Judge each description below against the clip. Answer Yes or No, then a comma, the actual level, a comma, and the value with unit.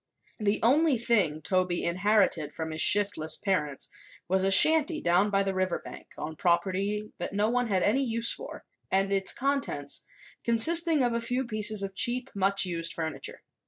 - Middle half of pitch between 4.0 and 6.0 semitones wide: Yes, average, 4.3 semitones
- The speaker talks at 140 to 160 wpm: No, average, 170 wpm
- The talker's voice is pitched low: No, high, 200 Hz